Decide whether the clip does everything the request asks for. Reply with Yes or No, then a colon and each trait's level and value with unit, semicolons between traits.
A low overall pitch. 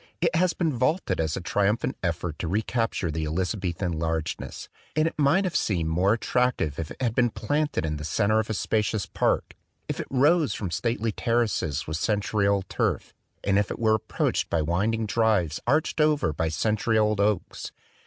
Yes: low, 105 Hz